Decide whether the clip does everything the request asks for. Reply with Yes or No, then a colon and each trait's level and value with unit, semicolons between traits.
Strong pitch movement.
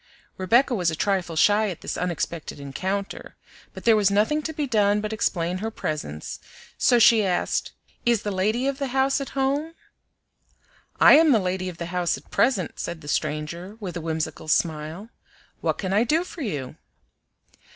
Yes: wide, 5.7 semitones